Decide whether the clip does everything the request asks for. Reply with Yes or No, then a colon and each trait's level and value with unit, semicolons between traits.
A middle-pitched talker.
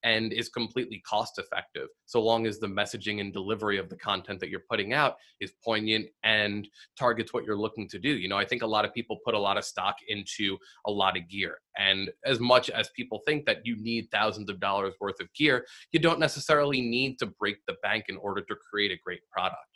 No: low, 110 Hz